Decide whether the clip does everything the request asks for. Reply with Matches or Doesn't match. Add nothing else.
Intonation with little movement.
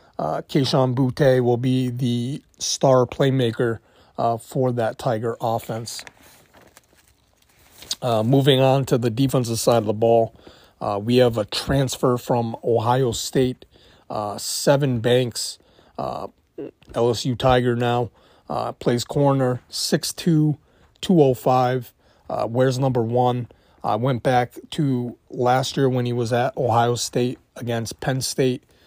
Matches